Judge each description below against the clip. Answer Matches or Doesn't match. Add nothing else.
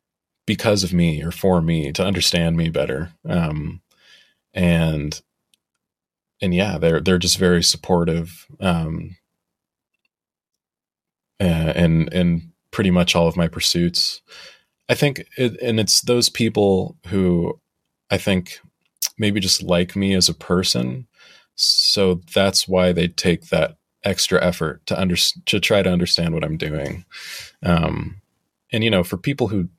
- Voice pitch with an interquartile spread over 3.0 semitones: Doesn't match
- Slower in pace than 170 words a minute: Matches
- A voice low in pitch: Matches